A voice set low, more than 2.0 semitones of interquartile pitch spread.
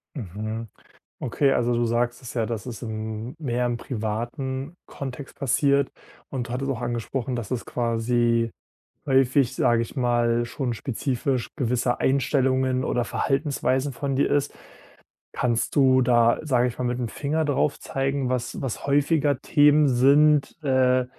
Yes: low, 125 Hz; narrow, 2.6 semitones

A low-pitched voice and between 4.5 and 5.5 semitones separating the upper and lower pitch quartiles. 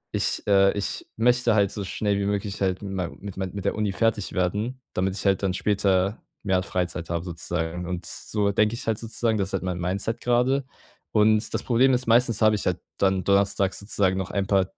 No: low, 100 Hz; narrow, 2.5 semitones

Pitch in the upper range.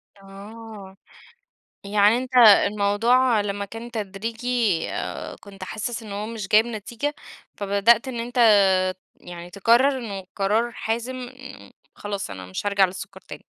Yes: high, 215 Hz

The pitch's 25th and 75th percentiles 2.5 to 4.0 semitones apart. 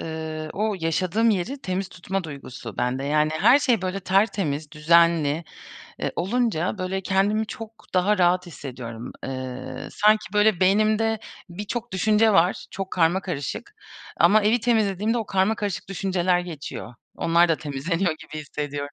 No: average, 5.1 semitones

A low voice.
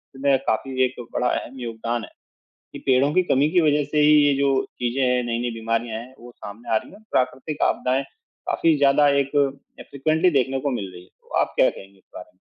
Yes: low, 130 Hz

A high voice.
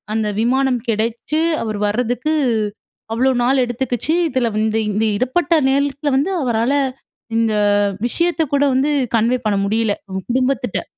Yes: high, 245 Hz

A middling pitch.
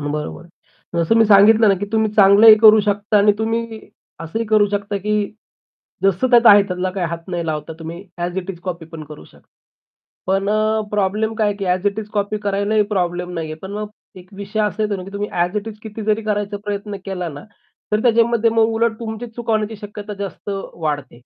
No: high, 205 Hz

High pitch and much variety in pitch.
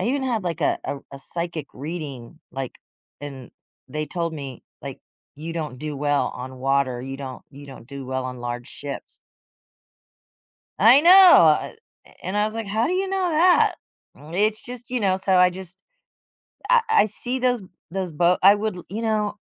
No: medium, 175 Hz; wide, 7.9 semitones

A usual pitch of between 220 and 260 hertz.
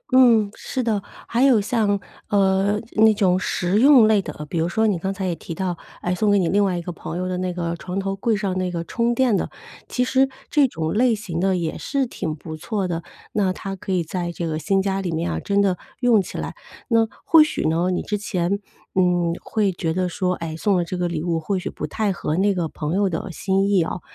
No: high, 190 Hz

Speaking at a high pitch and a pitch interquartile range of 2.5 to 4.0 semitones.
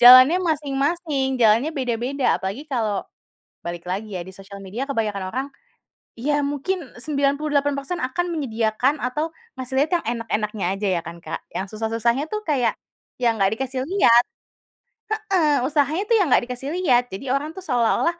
No: very high, 265 Hz; average, 5.0 semitones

